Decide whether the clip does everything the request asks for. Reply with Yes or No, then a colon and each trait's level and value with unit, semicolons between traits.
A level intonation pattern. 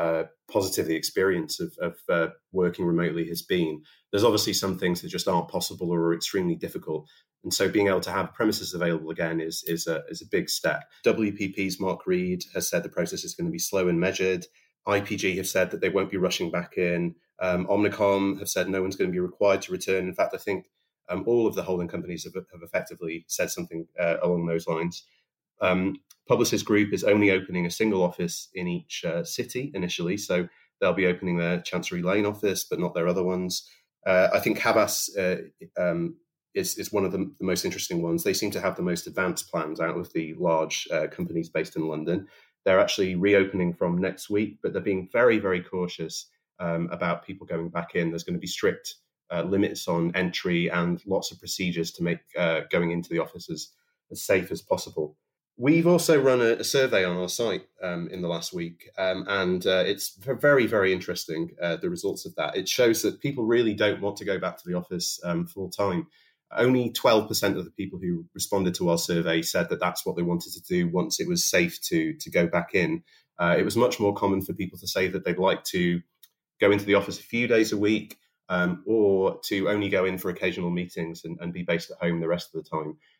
No: average, 3.3 semitones